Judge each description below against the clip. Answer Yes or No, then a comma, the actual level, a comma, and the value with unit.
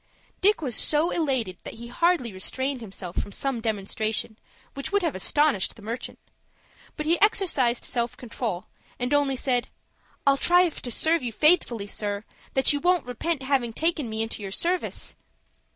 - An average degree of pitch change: No, wide, 5.7 semitones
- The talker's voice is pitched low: No, very high, 255 Hz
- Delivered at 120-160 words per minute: No, average, 170 wpm